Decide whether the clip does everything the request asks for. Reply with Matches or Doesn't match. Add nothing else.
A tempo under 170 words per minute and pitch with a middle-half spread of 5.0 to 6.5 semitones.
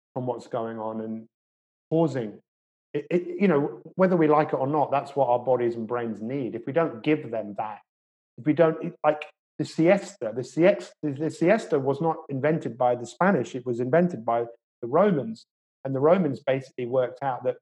Doesn't match